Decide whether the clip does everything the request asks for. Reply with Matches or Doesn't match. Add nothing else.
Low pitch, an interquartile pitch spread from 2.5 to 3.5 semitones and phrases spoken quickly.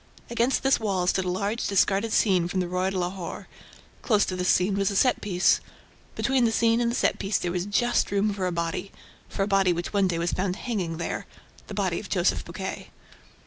Doesn't match